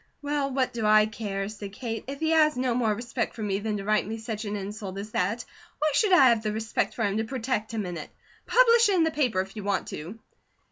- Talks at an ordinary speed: No, fast, 260 wpm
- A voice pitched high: Yes, high, 220 Hz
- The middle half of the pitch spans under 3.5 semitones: No, average, 4.1 semitones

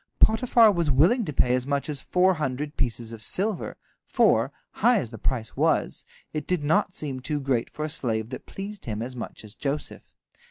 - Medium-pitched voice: Yes, medium, 145 Hz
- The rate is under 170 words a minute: No, average, 200 wpm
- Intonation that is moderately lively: No, wide, 6.3 semitones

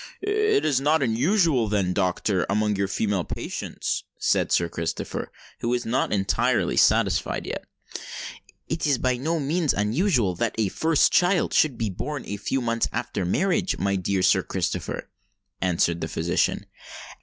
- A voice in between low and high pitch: No, low, 115 Hz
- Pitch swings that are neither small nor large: No, wide, 7.6 semitones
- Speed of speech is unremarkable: Yes, average, 155 wpm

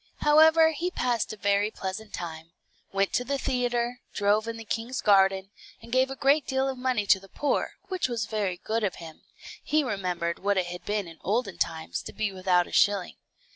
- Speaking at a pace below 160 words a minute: No, fast, 205 wpm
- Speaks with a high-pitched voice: Yes, high, 210 Hz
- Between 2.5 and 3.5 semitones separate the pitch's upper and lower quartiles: No, average, 4.8 semitones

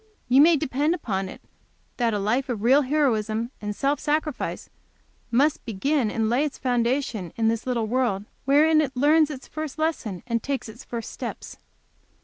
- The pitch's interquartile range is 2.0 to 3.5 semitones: No, average, 4.6 semitones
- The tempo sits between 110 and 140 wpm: No, average, 170 wpm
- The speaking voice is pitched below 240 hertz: No, very high, 255 Hz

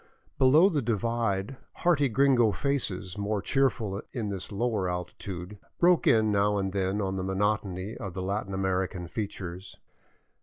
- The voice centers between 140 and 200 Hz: No, low, 100 Hz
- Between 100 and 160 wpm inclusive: Yes, average, 140 wpm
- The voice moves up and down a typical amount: Yes, average, 3.7 semitones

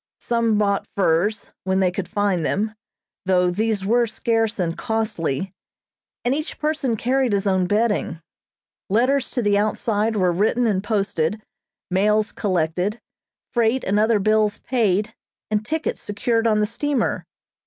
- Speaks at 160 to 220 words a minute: No, average, 145 wpm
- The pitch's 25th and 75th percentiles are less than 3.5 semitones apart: Yes, average, 3.0 semitones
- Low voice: No, high, 210 Hz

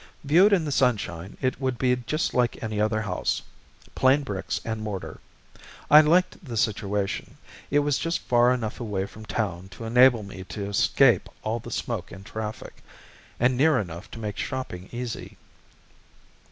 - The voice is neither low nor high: No, low, 115 Hz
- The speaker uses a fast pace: No, average, 165 wpm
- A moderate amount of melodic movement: Yes, average, 4.0 semitones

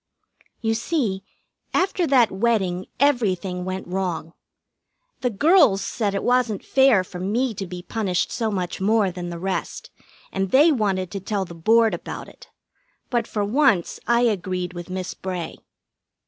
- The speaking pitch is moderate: No, high, 195 Hz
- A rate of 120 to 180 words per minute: Yes, average, 155 wpm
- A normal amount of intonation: Yes, average, 4.4 semitones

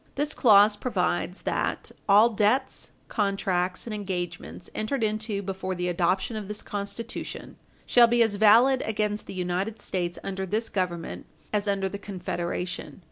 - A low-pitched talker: No, high, 200 Hz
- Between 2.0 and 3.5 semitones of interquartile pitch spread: Yes, average, 2.8 semitones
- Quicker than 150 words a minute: No, average, 145 wpm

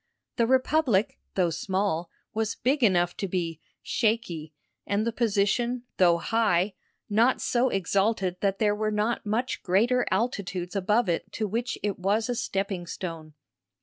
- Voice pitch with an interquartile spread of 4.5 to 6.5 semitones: No, average, 4.0 semitones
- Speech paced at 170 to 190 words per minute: No, average, 150 wpm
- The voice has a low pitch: No, high, 205 Hz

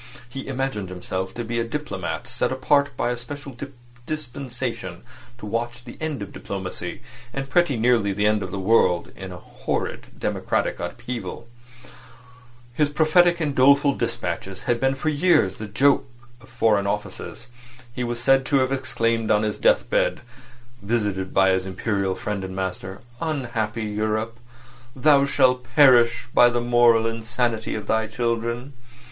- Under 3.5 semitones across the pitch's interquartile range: No, average, 4.2 semitones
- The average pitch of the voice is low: Yes, low, 120 Hz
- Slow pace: No, average, 150 wpm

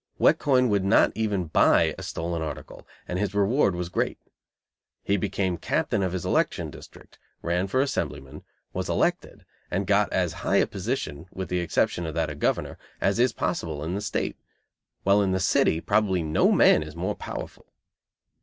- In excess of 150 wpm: Yes, average, 180 wpm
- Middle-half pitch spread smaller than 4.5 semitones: Yes, average, 3.3 semitones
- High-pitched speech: No, very low, 95 Hz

